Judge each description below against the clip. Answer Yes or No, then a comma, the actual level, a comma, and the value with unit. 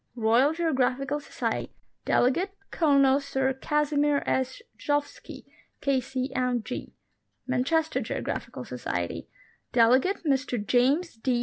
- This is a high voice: Yes, very high, 270 Hz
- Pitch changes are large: No, narrow, 2.6 semitones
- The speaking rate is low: Yes, slow, 85 wpm